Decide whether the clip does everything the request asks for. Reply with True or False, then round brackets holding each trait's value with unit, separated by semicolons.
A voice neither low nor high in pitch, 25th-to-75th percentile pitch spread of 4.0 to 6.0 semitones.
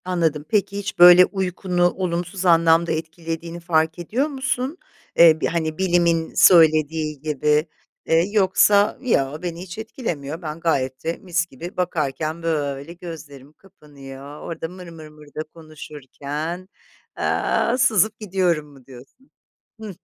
False (165 Hz; 3.1 semitones)